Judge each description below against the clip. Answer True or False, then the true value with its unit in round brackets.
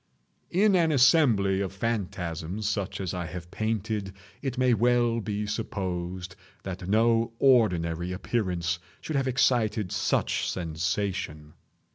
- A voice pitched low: True (100 Hz)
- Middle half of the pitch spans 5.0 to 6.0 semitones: False (4.6 semitones)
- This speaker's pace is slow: True (120 wpm)